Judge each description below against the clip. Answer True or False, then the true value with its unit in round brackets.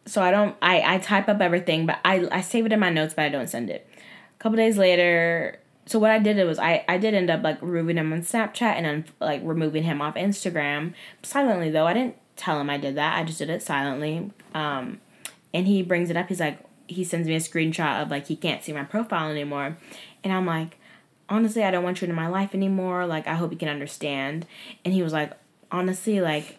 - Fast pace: True (240 wpm)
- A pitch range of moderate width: True (3.7 semitones)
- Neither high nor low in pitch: True (170 Hz)